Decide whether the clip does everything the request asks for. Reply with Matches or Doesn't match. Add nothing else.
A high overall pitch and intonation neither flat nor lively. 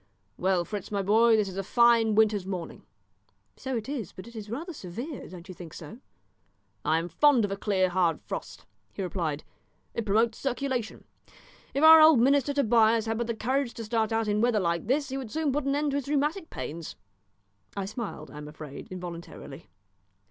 Doesn't match